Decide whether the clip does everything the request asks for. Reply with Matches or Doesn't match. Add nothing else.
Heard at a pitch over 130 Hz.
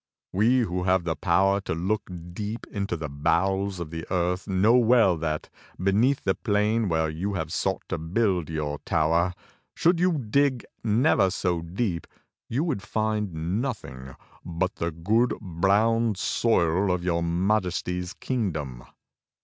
Doesn't match